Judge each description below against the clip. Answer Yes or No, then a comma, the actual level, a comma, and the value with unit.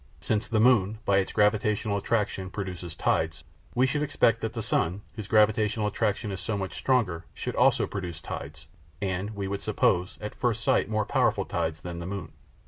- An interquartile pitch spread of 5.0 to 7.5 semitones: No, average, 2.7 semitones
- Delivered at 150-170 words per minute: No, average, 185 wpm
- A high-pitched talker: No, low, 100 Hz